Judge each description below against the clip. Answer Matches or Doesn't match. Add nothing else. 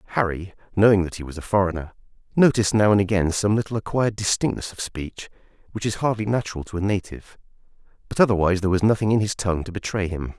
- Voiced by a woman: Doesn't match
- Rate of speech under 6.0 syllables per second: Doesn't match